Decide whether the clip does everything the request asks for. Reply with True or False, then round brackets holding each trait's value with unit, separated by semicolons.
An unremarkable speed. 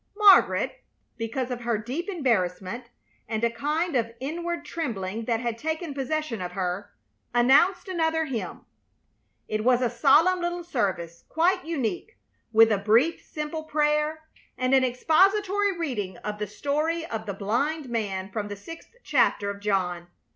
True (150 wpm)